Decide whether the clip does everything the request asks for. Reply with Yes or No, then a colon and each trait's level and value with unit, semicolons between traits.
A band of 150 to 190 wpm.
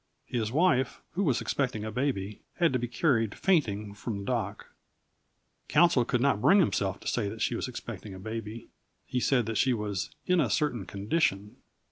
Yes: average, 185 wpm